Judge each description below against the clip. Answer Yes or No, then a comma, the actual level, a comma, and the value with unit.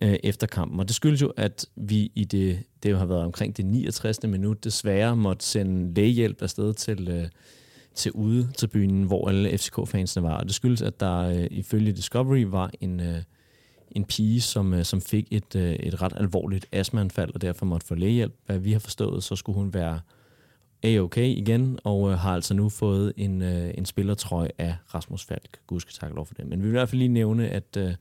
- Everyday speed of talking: Yes, average, 195 wpm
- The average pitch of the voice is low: Yes, low, 100 Hz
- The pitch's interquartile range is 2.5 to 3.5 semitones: Yes, average, 2.9 semitones